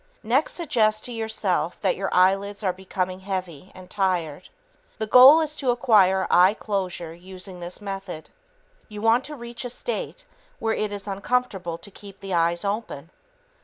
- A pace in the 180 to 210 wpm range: No, average, 165 wpm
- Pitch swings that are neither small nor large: Yes, average, 3.5 semitones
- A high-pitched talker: Yes, high, 195 Hz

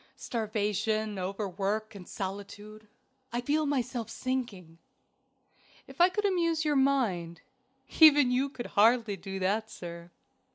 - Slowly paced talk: Yes, slow, 120 wpm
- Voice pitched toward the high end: Yes, high, 220 Hz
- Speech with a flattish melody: No, average, 5.1 semitones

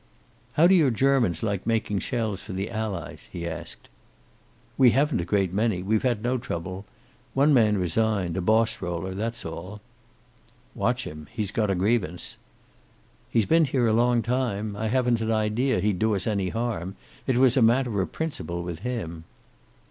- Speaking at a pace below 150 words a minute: No, average, 175 wpm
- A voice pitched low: Yes, low, 110 Hz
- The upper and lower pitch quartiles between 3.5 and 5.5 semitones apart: Yes, average, 4.3 semitones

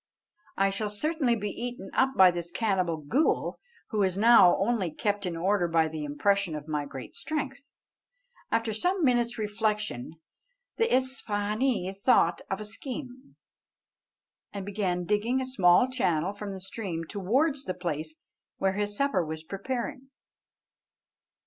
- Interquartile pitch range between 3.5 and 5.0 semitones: No, wide, 5.5 semitones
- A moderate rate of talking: Yes, average, 145 wpm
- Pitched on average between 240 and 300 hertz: No, high, 205 Hz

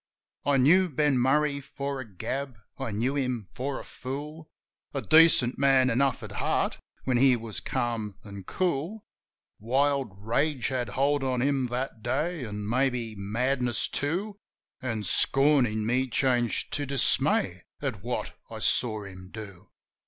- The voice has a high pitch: No, low, 130 Hz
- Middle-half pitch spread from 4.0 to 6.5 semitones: No, average, 3.5 semitones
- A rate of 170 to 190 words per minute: No, average, 155 wpm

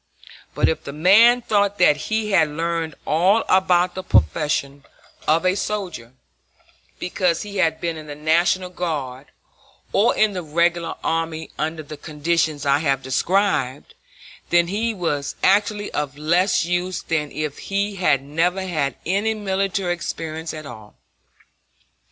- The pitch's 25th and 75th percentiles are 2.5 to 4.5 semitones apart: Yes, average, 3.9 semitones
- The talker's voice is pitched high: No, medium, 170 Hz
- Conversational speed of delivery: Yes, average, 145 wpm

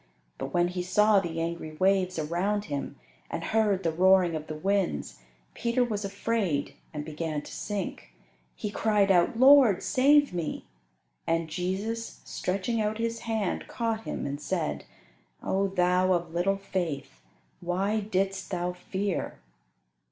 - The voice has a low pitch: No, high, 190 Hz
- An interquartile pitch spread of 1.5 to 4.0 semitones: Yes, average, 3.6 semitones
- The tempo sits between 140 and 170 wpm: Yes, average, 145 wpm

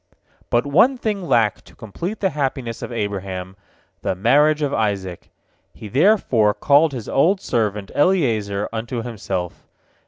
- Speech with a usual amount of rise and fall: No, wide, 6.6 semitones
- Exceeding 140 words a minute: No, slow, 135 wpm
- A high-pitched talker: No, low, 120 Hz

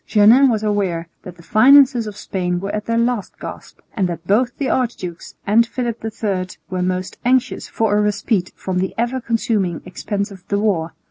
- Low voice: No, high, 210 Hz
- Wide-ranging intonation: No, average, 4.1 semitones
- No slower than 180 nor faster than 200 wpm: Yes, average, 190 wpm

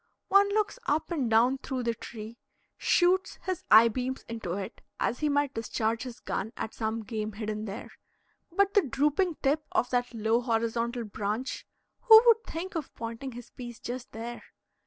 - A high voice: Yes, high, 245 Hz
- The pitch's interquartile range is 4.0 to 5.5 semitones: Yes, average, 5.0 semitones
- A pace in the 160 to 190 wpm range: Yes, average, 175 wpm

